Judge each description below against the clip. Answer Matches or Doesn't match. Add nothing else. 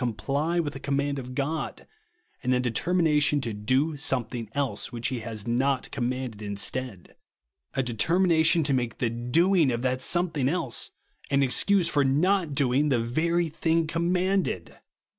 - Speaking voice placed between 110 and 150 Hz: Matches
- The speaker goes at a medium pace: Matches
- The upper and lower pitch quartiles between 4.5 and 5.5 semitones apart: Matches